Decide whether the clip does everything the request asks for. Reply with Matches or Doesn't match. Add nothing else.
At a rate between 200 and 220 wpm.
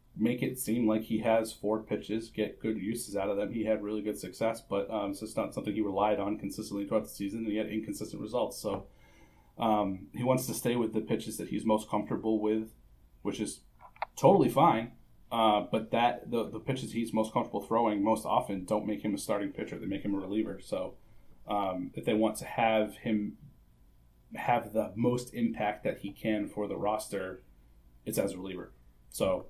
Matches